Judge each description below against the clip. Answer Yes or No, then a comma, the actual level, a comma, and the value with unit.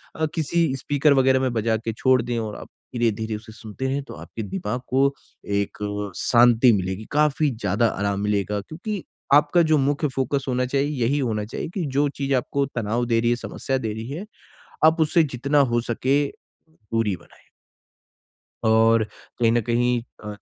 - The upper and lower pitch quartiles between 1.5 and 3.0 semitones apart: No, average, 4.1 semitones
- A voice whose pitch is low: Yes, low, 120 Hz